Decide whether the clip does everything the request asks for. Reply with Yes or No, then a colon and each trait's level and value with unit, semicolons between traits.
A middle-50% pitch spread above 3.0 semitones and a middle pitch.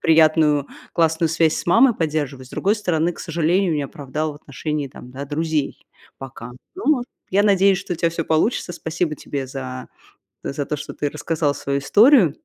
Yes: average, 3.4 semitones; medium, 155 Hz